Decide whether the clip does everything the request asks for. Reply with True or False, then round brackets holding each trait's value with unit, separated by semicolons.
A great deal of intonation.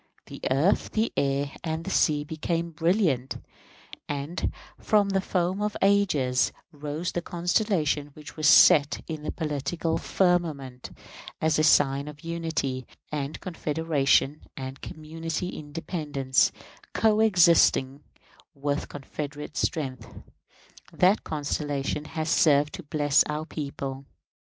False (3.1 semitones)